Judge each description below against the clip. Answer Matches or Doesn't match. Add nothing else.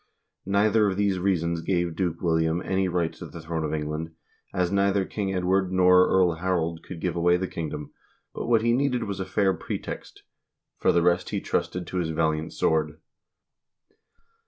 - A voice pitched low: Matches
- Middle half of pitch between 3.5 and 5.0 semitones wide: Doesn't match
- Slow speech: Doesn't match